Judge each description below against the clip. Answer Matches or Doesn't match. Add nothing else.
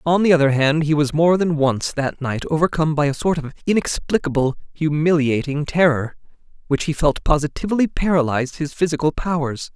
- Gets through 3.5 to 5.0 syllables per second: Doesn't match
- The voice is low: Doesn't match